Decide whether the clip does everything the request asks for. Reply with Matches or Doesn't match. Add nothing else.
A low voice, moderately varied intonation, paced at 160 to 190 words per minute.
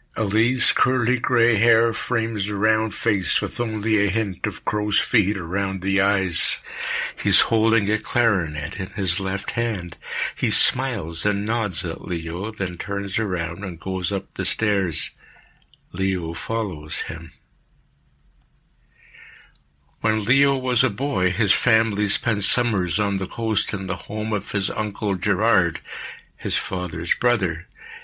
Doesn't match